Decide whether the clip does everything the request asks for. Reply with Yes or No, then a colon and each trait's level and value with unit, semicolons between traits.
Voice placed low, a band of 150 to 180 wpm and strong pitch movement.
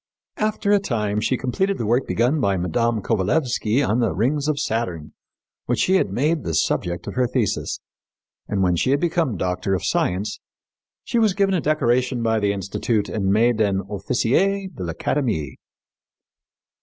Yes: low, 115 Hz; average, 165 wpm; wide, 6.7 semitones